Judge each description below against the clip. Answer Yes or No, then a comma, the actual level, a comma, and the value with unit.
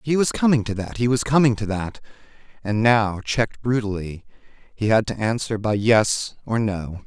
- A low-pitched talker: Yes, low, 110 Hz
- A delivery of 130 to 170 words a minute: No, average, 180 wpm